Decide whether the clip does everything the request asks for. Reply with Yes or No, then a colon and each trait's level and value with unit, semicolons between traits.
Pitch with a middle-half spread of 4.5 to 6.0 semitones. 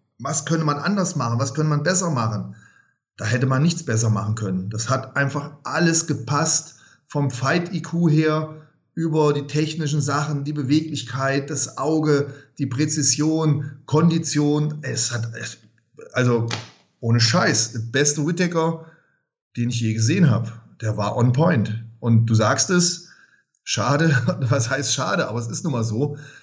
Yes: average, 4.8 semitones